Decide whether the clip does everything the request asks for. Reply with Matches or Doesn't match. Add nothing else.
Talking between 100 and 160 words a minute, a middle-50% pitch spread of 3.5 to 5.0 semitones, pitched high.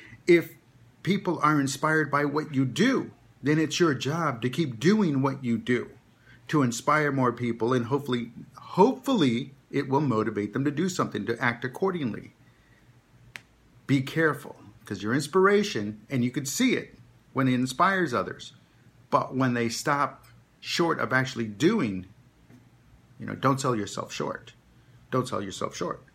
Doesn't match